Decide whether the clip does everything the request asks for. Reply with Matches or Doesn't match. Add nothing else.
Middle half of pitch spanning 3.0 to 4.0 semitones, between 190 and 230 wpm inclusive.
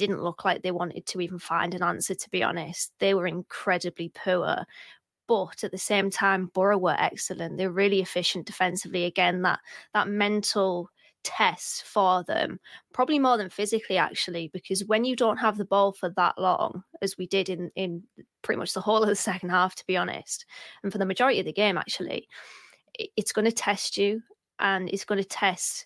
Doesn't match